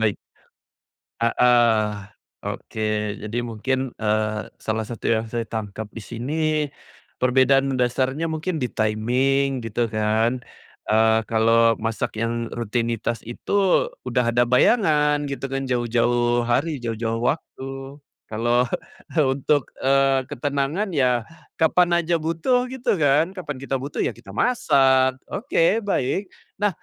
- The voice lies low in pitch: Yes, low, 125 Hz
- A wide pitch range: No, average, 4.0 semitones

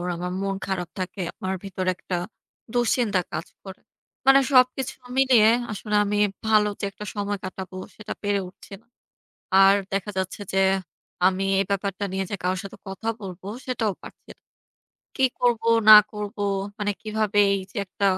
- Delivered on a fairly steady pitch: Yes, narrow, 2.3 semitones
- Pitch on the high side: Yes, high, 200 Hz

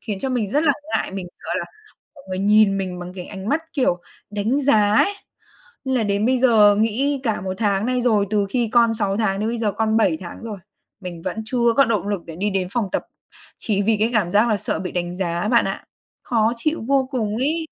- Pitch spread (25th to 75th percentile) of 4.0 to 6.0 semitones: No, average, 3.6 semitones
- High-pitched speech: Yes, high, 215 Hz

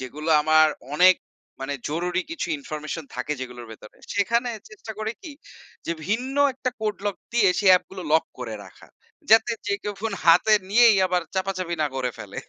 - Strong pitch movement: Yes, wide, 6.2 semitones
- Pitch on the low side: No, medium, 185 Hz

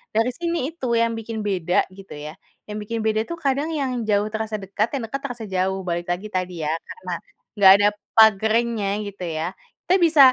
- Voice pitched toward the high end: Yes, high, 215 Hz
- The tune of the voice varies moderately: Yes, average, 3.7 semitones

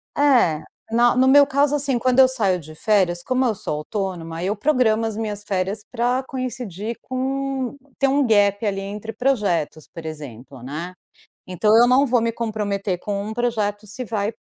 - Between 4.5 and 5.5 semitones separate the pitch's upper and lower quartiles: Yes, average, 4.9 semitones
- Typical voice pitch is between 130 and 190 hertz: No, high, 215 Hz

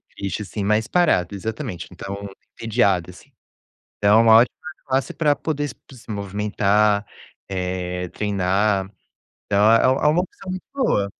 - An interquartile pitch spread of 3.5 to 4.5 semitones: Yes, average, 4.0 semitones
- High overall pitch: No, low, 105 Hz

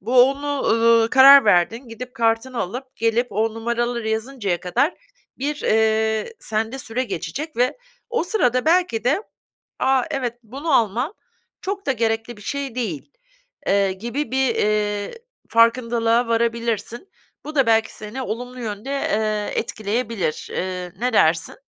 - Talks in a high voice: Yes, high, 230 Hz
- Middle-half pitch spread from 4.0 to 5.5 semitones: No, average, 3.0 semitones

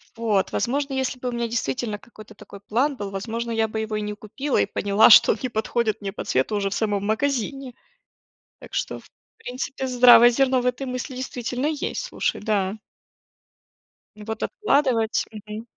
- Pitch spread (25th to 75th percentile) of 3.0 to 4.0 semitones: Yes, average, 3.3 semitones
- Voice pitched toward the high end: Yes, high, 230 Hz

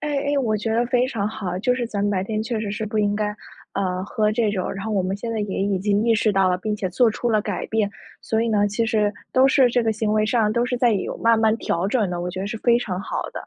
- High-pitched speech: Yes, high, 215 Hz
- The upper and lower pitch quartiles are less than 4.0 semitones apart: Yes, narrow, 2.4 semitones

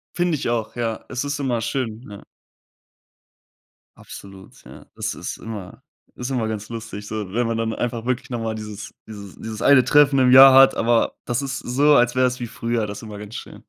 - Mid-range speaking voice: No, low, 115 Hz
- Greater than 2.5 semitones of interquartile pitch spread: Yes, average, 2.9 semitones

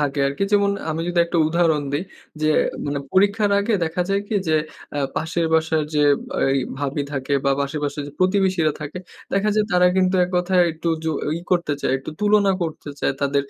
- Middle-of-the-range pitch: Yes, medium, 165 Hz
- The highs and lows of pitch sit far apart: No, average, 4.3 semitones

